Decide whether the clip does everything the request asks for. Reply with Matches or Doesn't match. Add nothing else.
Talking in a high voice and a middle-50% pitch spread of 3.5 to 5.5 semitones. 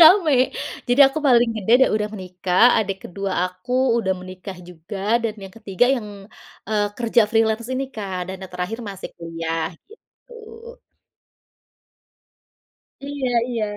Matches